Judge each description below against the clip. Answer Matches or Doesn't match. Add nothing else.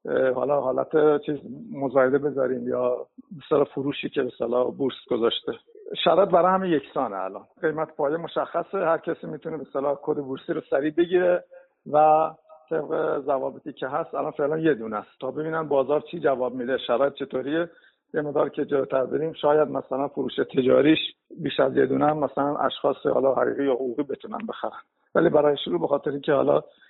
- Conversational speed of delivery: Doesn't match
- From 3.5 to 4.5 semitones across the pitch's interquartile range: Doesn't match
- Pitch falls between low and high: Matches